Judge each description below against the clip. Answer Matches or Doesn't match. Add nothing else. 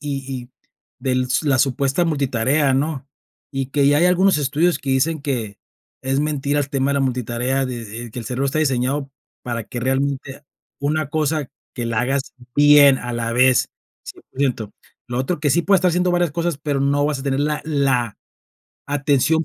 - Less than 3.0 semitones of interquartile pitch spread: Matches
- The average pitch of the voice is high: Doesn't match